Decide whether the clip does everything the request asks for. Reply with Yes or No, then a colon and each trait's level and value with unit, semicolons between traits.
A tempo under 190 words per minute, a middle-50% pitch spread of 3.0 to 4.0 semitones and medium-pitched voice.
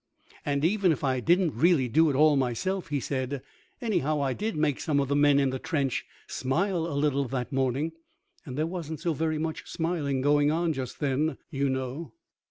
No: average, 195 wpm; average, 3.3 semitones; medium, 145 Hz